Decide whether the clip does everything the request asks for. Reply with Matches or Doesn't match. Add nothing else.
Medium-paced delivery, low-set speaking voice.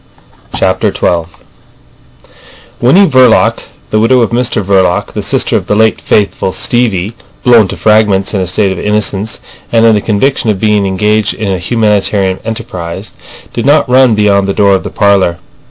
Matches